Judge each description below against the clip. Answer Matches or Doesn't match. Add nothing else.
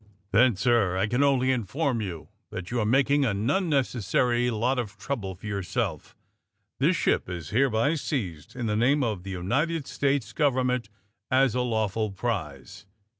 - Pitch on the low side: Matches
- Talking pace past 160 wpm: Matches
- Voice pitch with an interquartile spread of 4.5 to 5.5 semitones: Matches